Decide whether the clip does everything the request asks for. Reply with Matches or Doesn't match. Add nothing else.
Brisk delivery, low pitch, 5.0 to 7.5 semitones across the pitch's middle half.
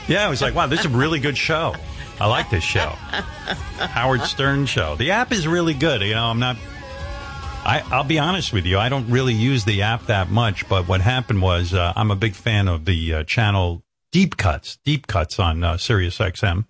Matches